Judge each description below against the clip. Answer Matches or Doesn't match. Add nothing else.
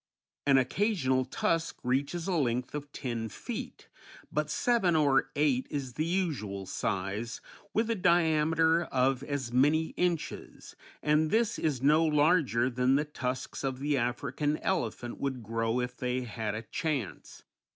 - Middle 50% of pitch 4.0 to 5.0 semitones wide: Matches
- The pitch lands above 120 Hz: Matches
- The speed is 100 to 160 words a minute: Matches